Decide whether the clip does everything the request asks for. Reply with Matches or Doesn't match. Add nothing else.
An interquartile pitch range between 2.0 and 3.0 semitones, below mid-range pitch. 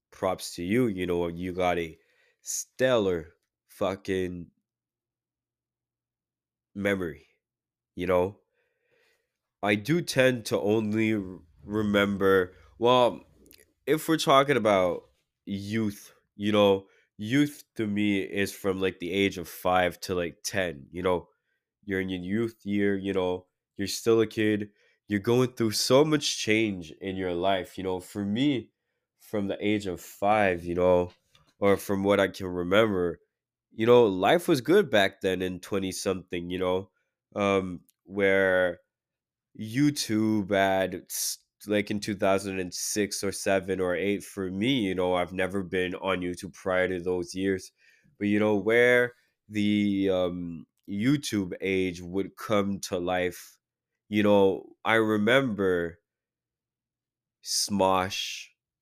Matches